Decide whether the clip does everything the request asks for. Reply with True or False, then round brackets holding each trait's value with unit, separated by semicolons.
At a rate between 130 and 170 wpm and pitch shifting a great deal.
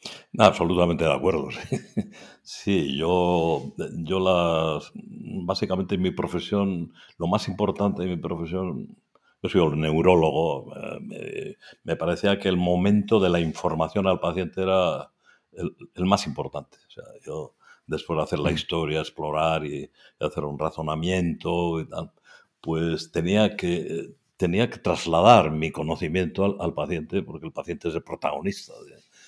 False (150 wpm; 2.9 semitones)